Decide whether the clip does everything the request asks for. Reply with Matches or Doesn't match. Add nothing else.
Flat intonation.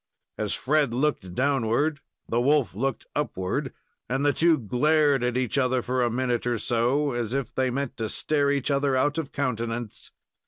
Doesn't match